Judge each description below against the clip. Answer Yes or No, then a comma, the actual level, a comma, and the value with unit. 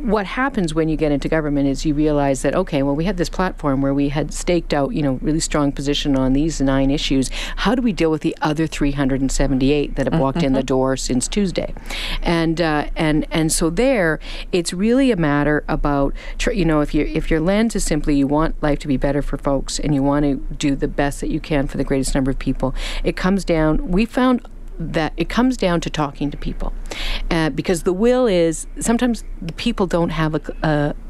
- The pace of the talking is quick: Yes, fast, 225 wpm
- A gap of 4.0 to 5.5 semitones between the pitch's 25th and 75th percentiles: No, average, 3.5 semitones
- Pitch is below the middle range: No, medium, 155 Hz